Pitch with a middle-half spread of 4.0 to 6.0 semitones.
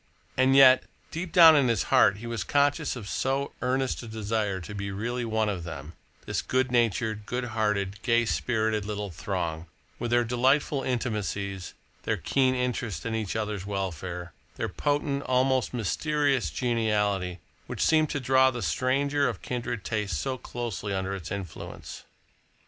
Yes: average, 4.5 semitones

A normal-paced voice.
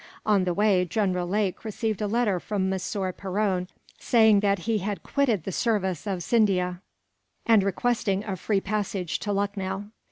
Yes: average, 160 wpm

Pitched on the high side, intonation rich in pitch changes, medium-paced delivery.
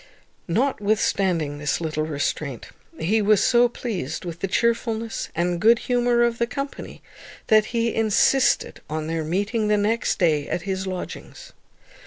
Yes: high, 205 Hz; wide, 5.9 semitones; average, 145 wpm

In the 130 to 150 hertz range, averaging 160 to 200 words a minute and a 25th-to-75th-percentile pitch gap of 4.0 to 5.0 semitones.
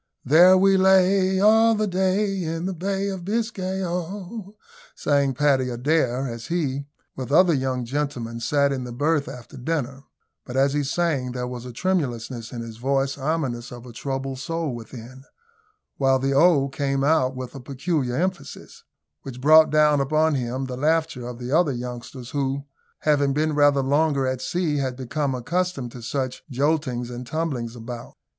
Yes: medium, 140 Hz; average, 170 wpm; average, 4.6 semitones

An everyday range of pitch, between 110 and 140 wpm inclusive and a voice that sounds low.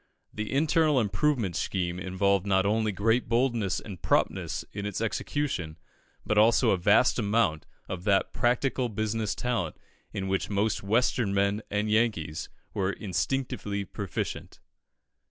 Yes: average, 3.3 semitones; slow, 135 wpm; low, 105 Hz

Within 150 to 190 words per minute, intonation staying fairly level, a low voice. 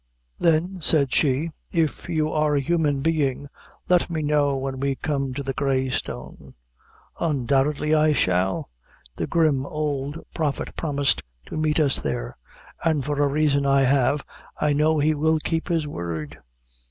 No: average, 155 wpm; narrow, 2.3 semitones; medium, 145 Hz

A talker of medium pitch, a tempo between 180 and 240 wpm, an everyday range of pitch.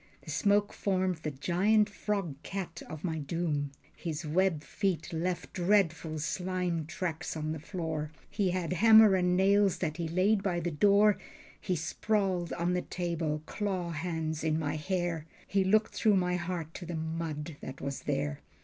No: medium, 175 Hz; average, 165 wpm; average, 3.2 semitones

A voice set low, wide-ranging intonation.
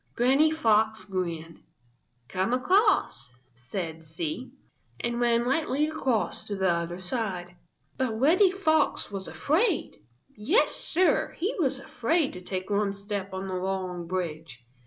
No: high, 210 Hz; wide, 7.0 semitones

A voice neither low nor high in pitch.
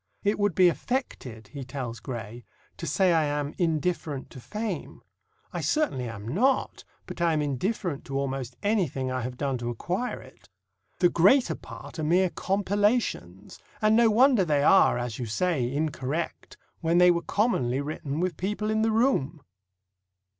Yes: medium, 160 Hz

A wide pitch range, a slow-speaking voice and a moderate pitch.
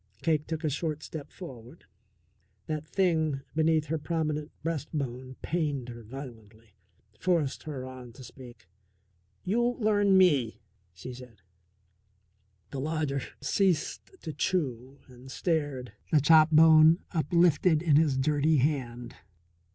No: average, 3.9 semitones; slow, 120 wpm; medium, 150 Hz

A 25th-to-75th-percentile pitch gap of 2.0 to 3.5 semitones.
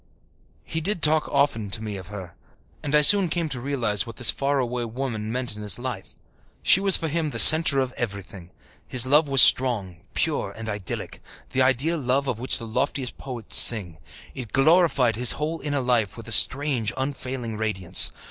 No: average, 4.6 semitones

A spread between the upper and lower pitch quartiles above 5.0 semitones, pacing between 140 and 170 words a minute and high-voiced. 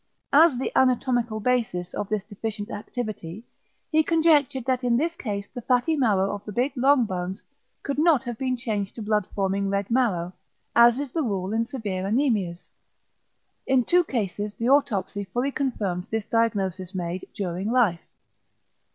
No: average, 4.7 semitones; average, 160 wpm; high, 225 Hz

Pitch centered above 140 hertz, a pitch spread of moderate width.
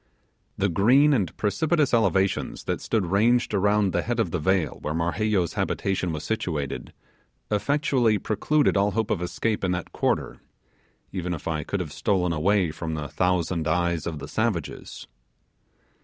No: very low, 95 Hz; average, 4.3 semitones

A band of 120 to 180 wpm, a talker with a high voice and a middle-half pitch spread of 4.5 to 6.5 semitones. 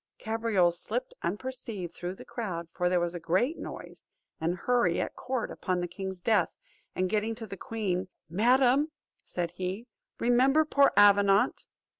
Yes: average, 155 wpm; high, 200 Hz; average, 5.2 semitones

